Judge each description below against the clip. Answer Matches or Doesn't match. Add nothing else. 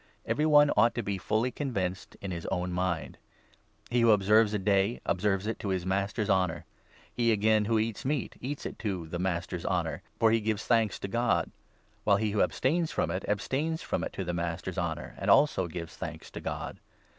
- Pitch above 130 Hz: Doesn't match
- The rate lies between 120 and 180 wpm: Doesn't match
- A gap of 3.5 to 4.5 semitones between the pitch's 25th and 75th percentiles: Matches